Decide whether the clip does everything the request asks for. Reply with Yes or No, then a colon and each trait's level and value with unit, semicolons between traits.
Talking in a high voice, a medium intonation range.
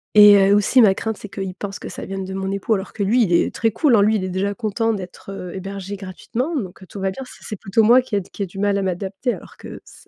No: high, 200 Hz; narrow, 2.3 semitones